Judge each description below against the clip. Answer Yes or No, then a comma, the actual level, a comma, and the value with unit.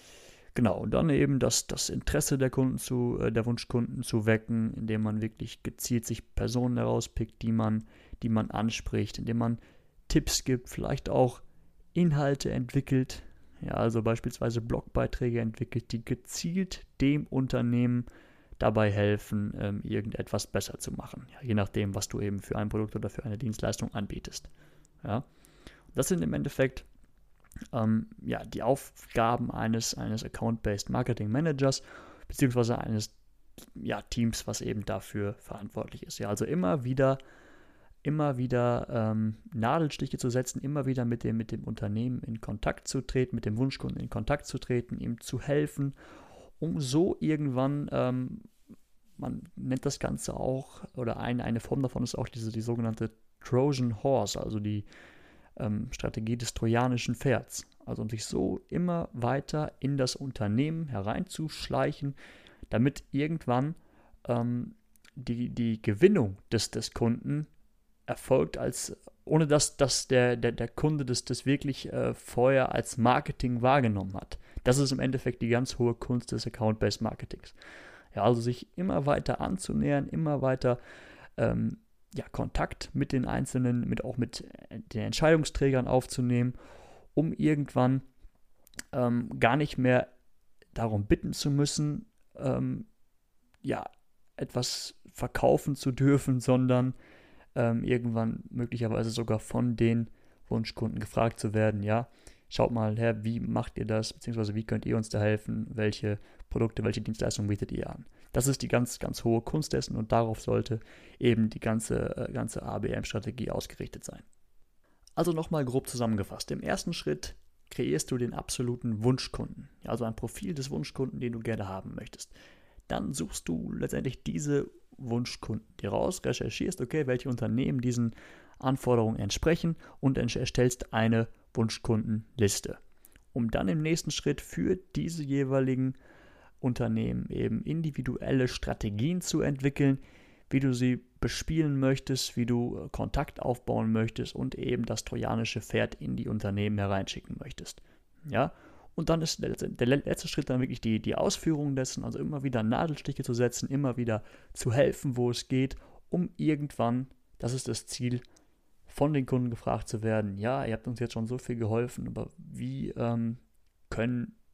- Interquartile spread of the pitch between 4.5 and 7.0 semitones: No, average, 3.1 semitones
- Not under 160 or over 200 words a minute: No, average, 150 wpm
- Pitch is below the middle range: Yes, low, 120 Hz